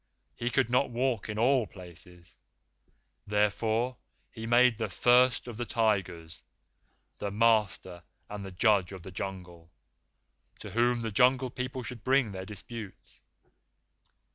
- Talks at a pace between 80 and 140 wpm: Yes, slow, 135 wpm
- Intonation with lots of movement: No, average, 4.3 semitones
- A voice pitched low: Yes, low, 110 Hz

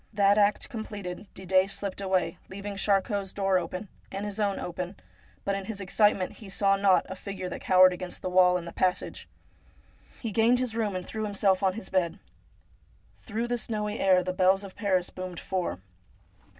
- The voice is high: Yes, high, 195 Hz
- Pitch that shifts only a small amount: Yes, narrow, 2.0 semitones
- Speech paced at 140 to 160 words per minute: No, average, 190 wpm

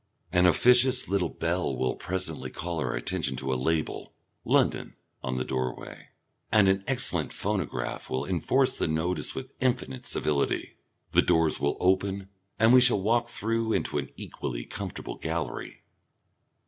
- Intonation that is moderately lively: No, wide, 7.0 semitones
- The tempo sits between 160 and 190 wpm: No, average, 150 wpm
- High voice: No, very low, 90 Hz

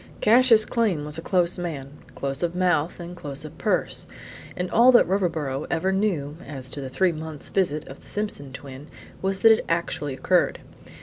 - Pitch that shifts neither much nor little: Yes, average, 4.8 semitones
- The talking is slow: No, average, 185 wpm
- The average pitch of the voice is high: No, medium, 170 Hz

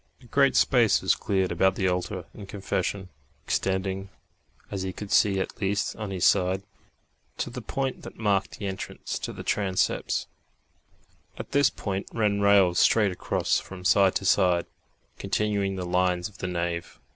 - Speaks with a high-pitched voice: No, very low, 95 Hz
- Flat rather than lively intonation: Yes, narrow, 1.9 semitones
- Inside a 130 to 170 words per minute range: Yes, average, 165 wpm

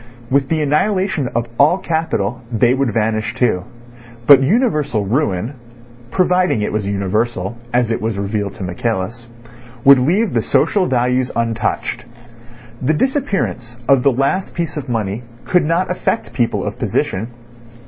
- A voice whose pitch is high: No, low, 125 Hz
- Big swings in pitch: Yes, wide, 6.0 semitones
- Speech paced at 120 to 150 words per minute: Yes, average, 145 wpm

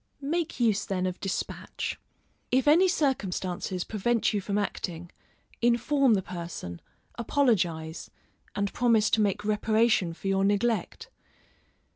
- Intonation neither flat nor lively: Yes, average, 4.4 semitones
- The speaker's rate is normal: No, slow, 120 wpm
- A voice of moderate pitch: No, high, 210 Hz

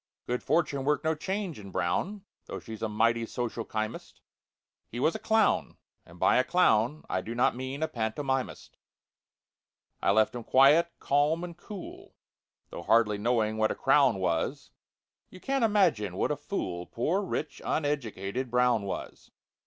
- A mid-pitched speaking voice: No, low, 125 Hz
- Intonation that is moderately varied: No, wide, 6.4 semitones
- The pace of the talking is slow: No, average, 155 wpm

